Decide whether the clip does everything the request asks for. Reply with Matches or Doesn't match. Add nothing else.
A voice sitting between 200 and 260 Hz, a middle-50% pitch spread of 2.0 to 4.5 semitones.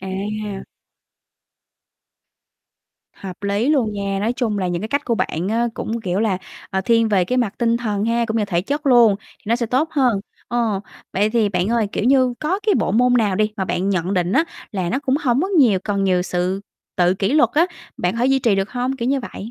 Matches